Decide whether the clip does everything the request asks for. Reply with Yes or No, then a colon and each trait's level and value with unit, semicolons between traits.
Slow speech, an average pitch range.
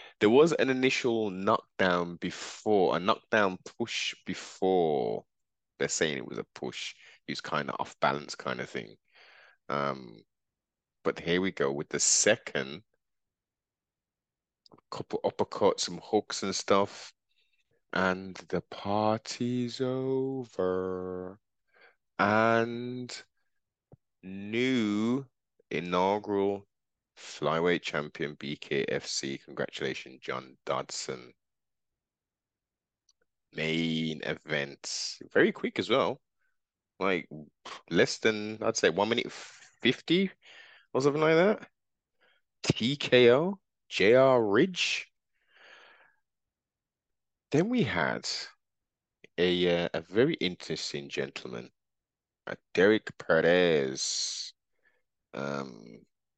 No: slow, 90 wpm; wide, 5.7 semitones